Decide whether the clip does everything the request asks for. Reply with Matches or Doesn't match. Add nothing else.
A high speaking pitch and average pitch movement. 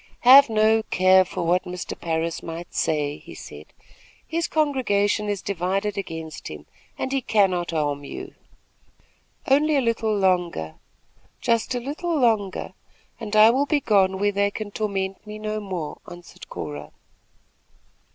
Matches